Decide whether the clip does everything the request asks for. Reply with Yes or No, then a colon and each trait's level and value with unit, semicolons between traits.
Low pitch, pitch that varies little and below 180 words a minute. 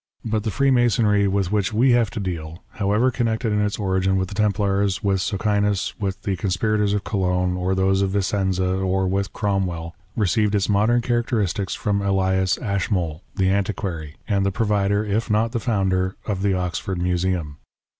Yes: low, 100 Hz; narrow, 2.1 semitones; average, 170 wpm